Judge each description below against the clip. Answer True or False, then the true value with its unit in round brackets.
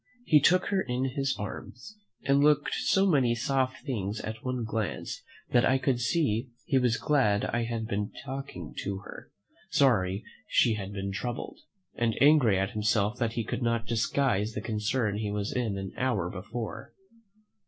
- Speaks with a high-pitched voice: False (120 Hz)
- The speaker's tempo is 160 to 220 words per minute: True (170 wpm)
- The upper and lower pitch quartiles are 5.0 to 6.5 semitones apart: False (4.1 semitones)